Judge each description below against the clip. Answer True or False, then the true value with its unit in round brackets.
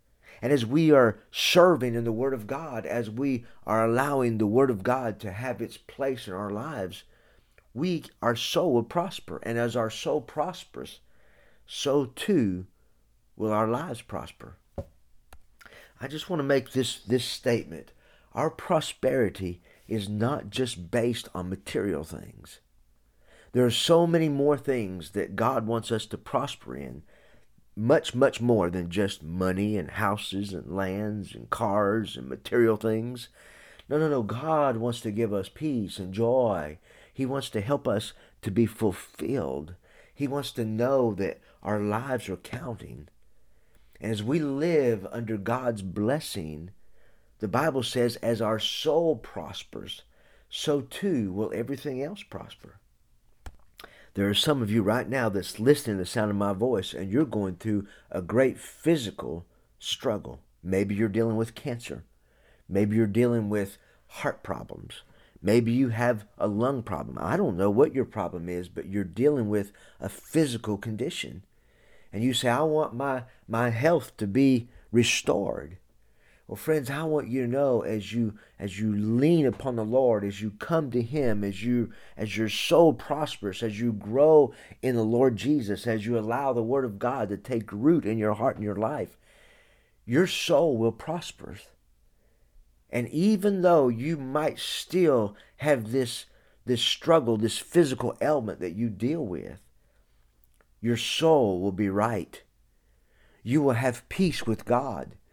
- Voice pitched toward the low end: True (115 Hz)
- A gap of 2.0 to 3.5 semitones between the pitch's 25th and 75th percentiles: False (4.3 semitones)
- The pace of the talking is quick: False (160 wpm)